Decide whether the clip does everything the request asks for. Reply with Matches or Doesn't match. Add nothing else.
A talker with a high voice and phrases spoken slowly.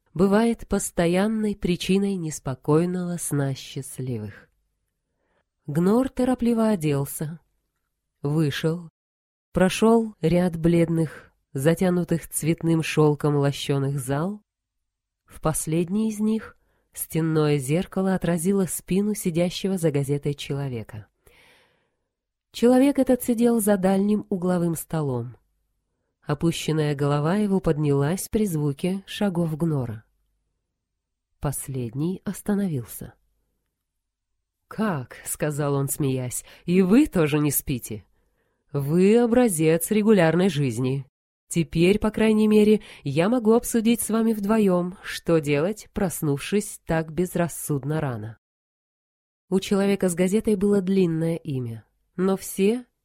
Doesn't match